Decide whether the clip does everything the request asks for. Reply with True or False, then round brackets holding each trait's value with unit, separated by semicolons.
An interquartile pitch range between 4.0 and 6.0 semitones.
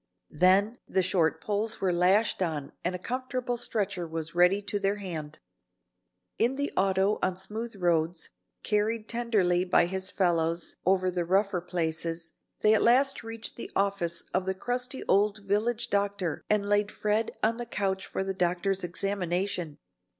False (3.2 semitones)